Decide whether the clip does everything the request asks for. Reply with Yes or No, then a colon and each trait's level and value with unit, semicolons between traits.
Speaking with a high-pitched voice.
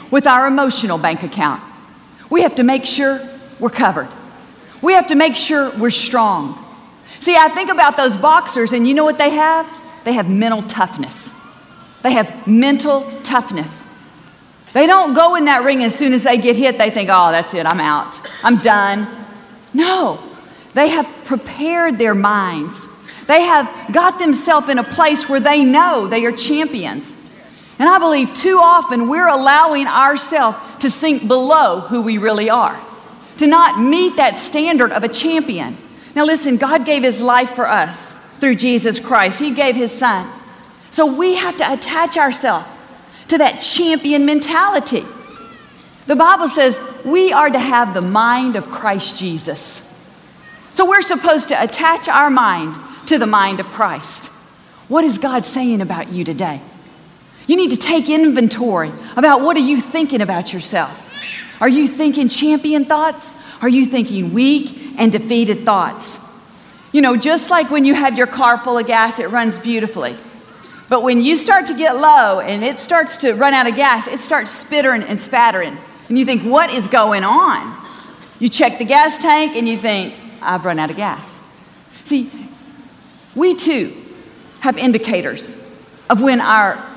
Yes: very high, 265 Hz